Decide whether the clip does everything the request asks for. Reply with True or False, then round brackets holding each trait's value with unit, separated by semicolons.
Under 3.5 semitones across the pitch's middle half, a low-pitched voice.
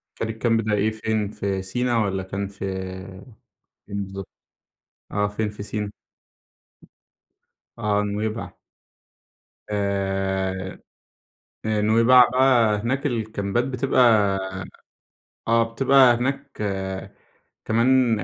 True (3.1 semitones; 110 Hz)